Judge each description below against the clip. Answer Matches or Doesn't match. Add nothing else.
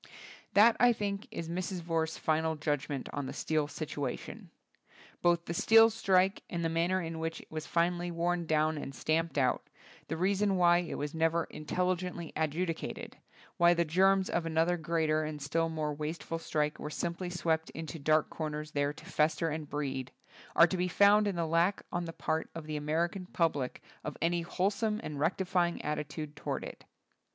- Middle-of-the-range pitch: Matches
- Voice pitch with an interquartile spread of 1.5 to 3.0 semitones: Matches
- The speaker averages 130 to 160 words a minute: Doesn't match